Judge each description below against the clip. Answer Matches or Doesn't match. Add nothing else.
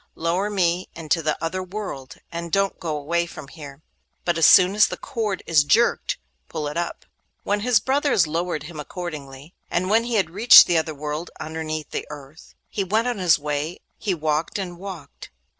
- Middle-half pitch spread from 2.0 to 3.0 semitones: Doesn't match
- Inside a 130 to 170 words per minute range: Doesn't match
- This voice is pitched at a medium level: Matches